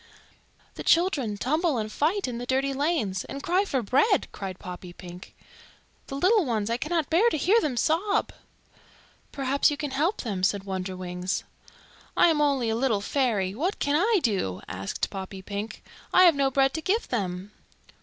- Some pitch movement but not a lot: No, wide, 8.0 semitones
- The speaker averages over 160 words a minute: Yes, average, 170 wpm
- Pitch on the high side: Yes, very high, 265 Hz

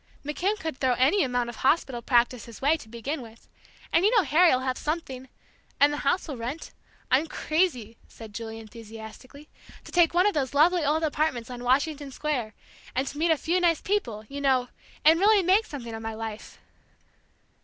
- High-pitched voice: Yes, very high, 275 Hz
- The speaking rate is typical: Yes, average, 185 wpm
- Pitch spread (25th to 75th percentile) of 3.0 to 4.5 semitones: No, average, 5.2 semitones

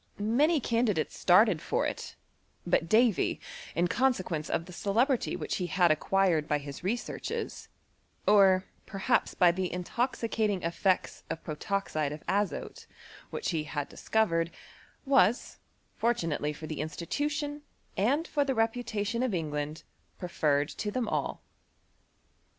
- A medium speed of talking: No, slow, 130 wpm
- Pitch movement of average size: No, wide, 6.0 semitones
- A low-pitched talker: No, high, 190 Hz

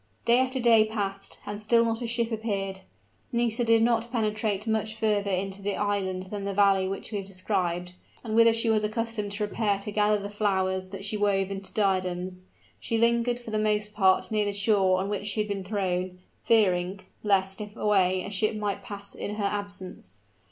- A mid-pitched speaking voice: No, high, 205 Hz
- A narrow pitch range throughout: Yes, narrow, 2.3 semitones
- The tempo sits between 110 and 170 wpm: No, average, 200 wpm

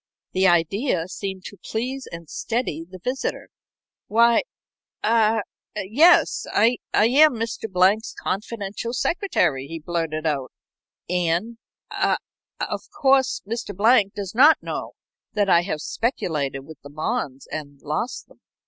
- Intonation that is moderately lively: No, wide, 6.1 semitones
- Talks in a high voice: Yes, high, 200 Hz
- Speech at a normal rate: No, slow, 130 wpm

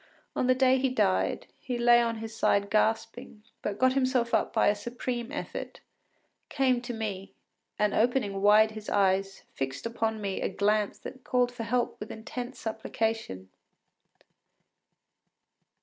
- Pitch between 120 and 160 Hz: No, high, 225 Hz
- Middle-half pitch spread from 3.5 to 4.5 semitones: No, average, 3.0 semitones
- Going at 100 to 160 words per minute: Yes, average, 150 wpm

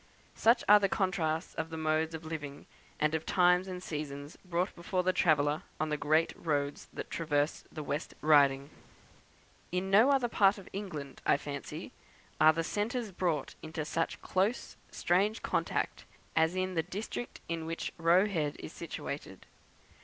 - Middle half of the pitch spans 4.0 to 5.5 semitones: No, average, 3.5 semitones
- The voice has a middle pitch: Yes, medium, 165 Hz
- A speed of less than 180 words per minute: Yes, average, 160 wpm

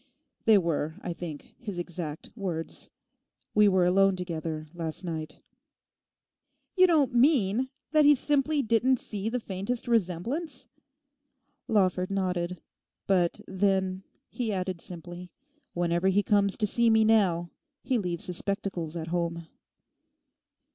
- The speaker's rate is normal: No, slow, 125 wpm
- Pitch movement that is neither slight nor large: Yes, average, 4.4 semitones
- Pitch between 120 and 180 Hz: No, high, 190 Hz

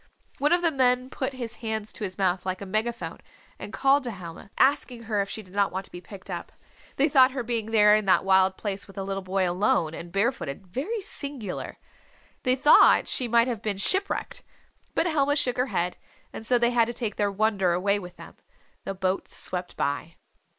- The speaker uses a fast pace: Yes, fast, 215 wpm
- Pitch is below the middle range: No, high, 215 Hz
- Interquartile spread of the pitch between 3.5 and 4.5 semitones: No, average, 4.9 semitones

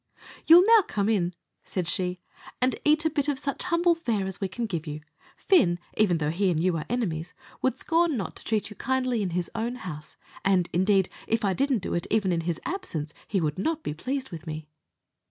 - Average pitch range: No, wide, 7.2 semitones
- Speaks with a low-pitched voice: No, high, 200 Hz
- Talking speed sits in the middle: No, fast, 220 wpm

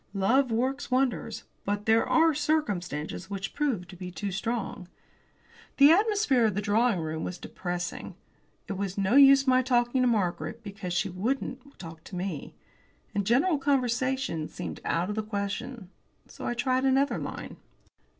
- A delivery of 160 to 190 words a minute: No, average, 150 wpm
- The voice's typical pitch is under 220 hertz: No, high, 225 Hz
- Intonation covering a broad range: Yes, wide, 5.7 semitones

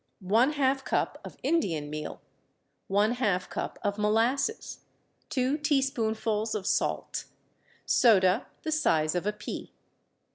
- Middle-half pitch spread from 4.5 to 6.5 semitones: Yes, wide, 5.4 semitones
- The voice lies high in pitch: Yes, high, 220 Hz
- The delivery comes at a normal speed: No, slow, 120 wpm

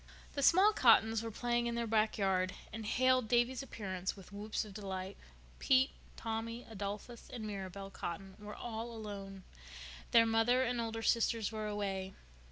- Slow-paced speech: No, average, 160 wpm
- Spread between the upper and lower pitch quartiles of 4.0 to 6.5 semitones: No, average, 3.0 semitones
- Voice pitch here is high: Yes, high, 220 Hz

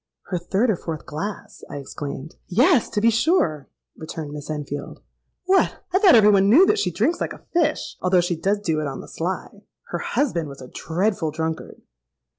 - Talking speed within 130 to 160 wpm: No, average, 190 wpm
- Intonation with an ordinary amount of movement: No, wide, 6.6 semitones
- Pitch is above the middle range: No, medium, 180 Hz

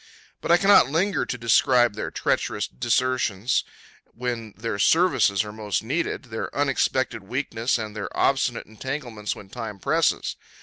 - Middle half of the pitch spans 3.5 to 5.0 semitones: Yes, average, 4.1 semitones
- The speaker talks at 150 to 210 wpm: No, average, 140 wpm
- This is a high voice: No, low, 120 Hz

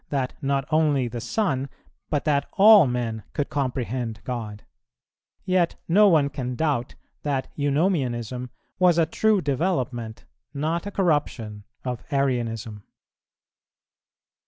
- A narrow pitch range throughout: No, average, 4.7 semitones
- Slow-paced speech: Yes, slow, 115 wpm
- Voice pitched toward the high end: No, medium, 140 Hz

